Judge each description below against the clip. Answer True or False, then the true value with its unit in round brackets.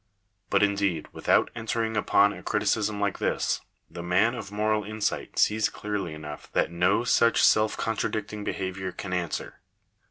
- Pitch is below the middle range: True (105 Hz)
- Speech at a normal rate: True (150 wpm)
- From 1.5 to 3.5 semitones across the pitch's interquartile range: True (2.7 semitones)